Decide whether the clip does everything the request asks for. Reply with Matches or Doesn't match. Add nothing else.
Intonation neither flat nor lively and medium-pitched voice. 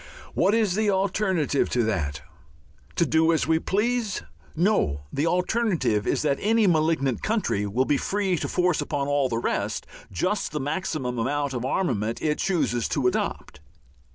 Doesn't match